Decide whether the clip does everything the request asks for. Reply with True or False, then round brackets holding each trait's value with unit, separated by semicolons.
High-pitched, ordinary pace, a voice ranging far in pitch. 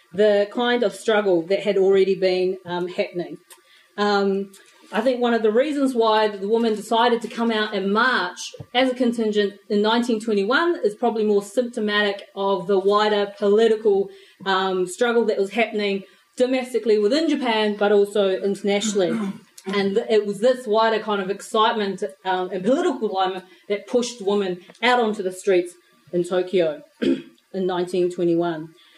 False (205 Hz; 150 wpm; 2.9 semitones)